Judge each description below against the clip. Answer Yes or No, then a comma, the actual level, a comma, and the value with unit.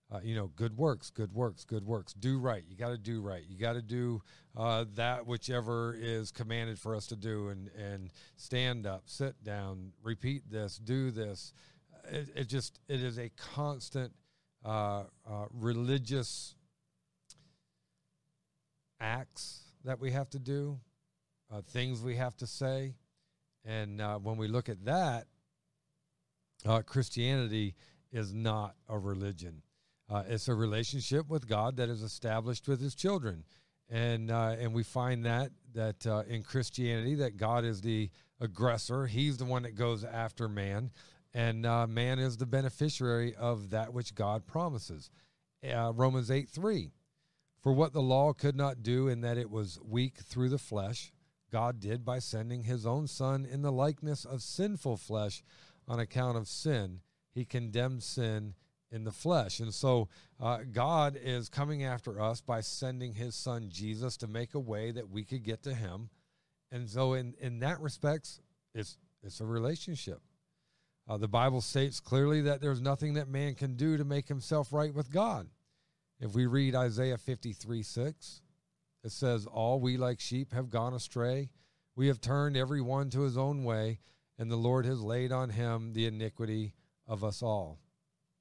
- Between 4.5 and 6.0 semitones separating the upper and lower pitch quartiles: No, average, 3.6 semitones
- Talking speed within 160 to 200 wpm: Yes, average, 170 wpm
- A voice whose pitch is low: Yes, low, 125 Hz